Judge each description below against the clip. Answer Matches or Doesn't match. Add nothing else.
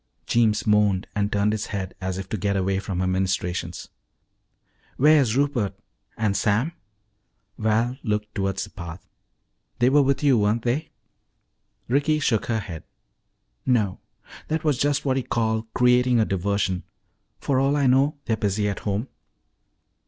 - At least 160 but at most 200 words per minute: Doesn't match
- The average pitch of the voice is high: Doesn't match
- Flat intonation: Doesn't match